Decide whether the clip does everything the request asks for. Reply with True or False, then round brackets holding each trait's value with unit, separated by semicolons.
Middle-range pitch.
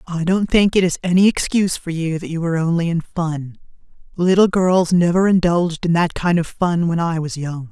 True (175 Hz)